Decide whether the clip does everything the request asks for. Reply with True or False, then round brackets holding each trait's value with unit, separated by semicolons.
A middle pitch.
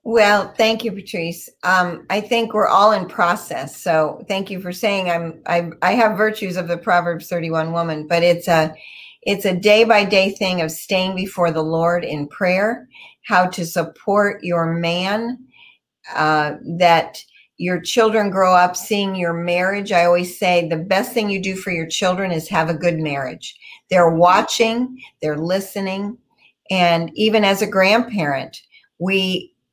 True (180 Hz)